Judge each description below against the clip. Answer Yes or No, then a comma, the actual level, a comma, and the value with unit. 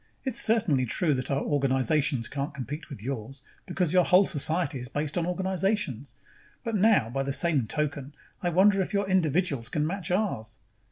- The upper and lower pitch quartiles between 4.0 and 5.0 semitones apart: No, wide, 5.4 semitones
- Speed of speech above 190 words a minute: No, average, 175 wpm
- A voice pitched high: No, medium, 150 Hz